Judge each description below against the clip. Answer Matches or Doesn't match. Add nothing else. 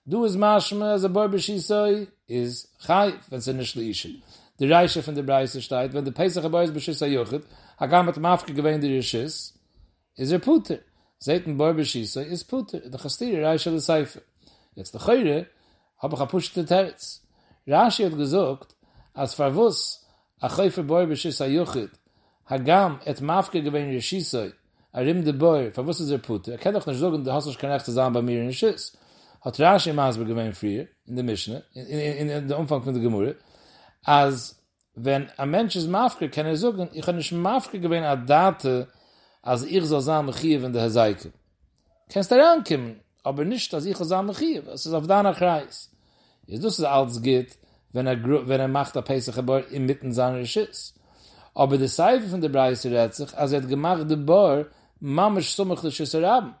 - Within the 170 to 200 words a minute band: Matches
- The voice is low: Doesn't match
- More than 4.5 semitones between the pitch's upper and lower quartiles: Matches